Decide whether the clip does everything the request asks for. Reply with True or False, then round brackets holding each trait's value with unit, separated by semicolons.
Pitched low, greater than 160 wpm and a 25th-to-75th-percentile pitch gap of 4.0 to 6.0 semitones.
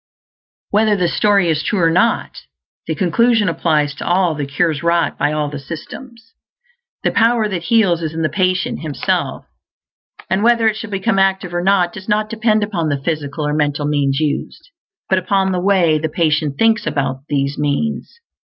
False (175 Hz; 180 wpm; 5.5 semitones)